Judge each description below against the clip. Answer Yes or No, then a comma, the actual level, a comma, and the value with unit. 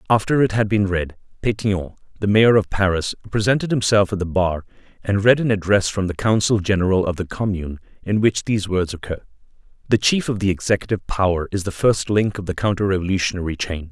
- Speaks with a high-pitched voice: No, low, 100 Hz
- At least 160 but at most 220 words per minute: Yes, average, 200 wpm